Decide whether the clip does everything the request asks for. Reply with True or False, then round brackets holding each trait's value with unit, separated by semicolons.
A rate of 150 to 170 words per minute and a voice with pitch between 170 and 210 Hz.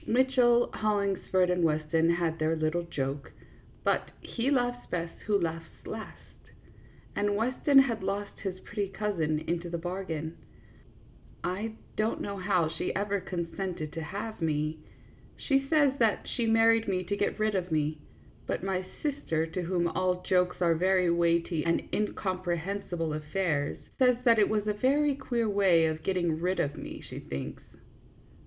True (160 wpm; 185 Hz)